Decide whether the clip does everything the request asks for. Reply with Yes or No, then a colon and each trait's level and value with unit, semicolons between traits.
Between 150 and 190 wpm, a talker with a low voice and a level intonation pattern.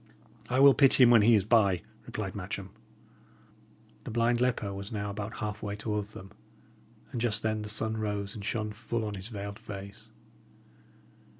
Yes: average, 170 wpm; low, 105 Hz; narrow, 2.3 semitones